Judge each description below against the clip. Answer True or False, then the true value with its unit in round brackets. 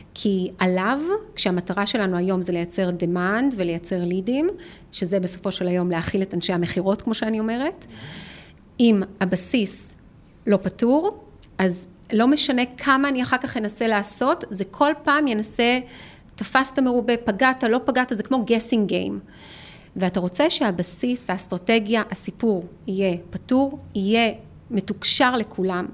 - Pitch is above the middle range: True (210 Hz)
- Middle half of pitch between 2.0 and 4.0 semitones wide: False (5.2 semitones)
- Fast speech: False (130 wpm)